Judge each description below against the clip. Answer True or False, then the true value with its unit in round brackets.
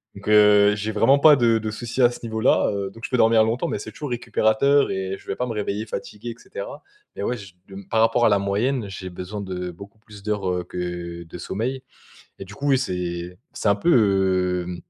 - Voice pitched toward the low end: True (105 Hz)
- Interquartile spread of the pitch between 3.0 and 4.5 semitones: True (3.4 semitones)